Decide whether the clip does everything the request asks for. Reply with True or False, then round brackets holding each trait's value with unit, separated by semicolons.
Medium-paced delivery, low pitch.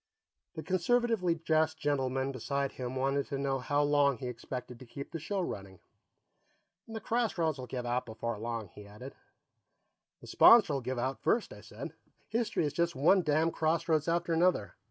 False (170 wpm; 145 Hz)